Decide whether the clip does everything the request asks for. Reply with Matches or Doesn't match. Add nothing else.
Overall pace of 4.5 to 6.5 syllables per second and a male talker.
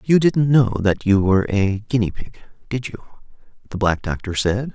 Matches